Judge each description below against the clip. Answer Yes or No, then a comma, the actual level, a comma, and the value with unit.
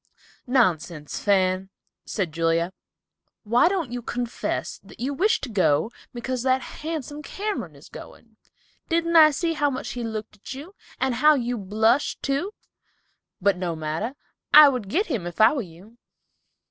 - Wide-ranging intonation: Yes, wide, 7.2 semitones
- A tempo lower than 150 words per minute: No, average, 160 wpm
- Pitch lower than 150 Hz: No, high, 240 Hz